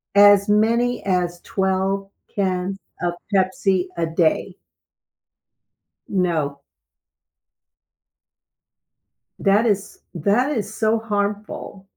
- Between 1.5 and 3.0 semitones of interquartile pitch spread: Yes, narrow, 2.4 semitones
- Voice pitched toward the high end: Yes, high, 195 Hz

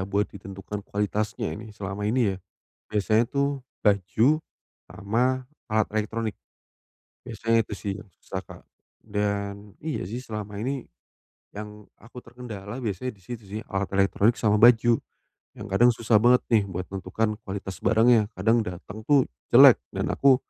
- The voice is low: Yes, low, 105 Hz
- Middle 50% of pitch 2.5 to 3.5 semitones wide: Yes, average, 2.8 semitones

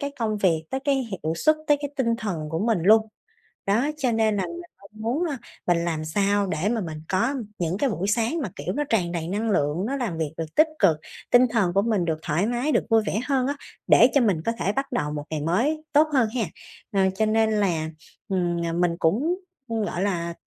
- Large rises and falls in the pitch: Yes, wide, 6.0 semitones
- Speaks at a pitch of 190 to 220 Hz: Yes, high, 210 Hz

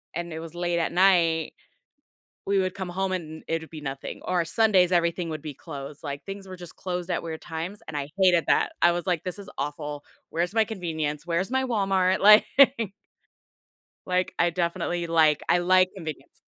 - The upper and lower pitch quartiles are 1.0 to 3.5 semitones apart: Yes, narrow, 2.6 semitones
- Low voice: No, medium, 175 Hz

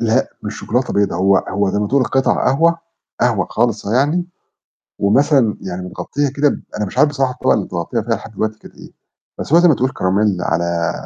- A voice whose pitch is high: No, low, 115 Hz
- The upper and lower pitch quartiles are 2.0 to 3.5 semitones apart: No, average, 5.3 semitones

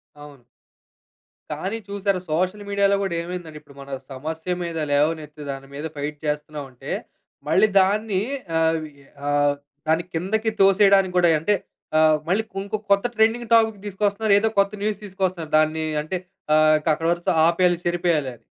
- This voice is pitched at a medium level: Yes, medium, 175 Hz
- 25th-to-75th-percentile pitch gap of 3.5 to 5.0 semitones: Yes, average, 4.5 semitones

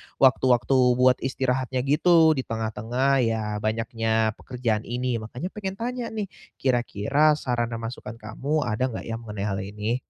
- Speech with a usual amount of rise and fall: Yes, average, 3.2 semitones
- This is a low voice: Yes, low, 125 Hz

